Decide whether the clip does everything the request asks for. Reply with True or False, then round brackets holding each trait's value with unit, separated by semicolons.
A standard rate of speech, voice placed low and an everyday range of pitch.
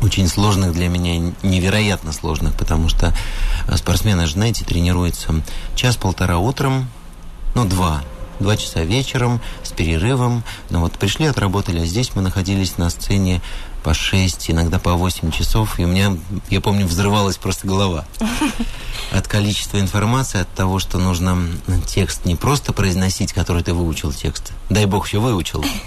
True (145 wpm; 95 Hz; 3.2 semitones)